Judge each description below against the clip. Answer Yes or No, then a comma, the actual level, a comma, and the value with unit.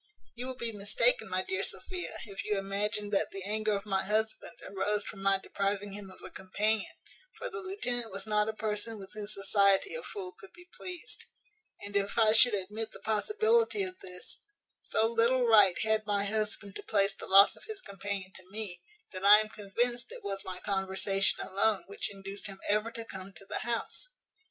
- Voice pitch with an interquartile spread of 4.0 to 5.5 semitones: No, average, 2.7 semitones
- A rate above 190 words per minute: Yes, average, 200 wpm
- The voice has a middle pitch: No, high, 210 Hz